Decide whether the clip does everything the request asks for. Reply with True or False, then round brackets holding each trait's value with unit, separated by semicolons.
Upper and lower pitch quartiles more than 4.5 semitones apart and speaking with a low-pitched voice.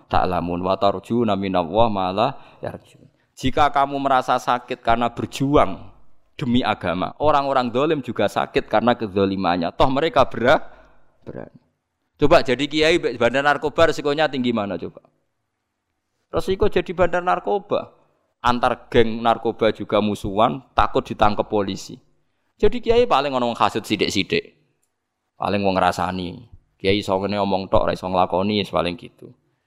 True (5.3 semitones; 115 Hz)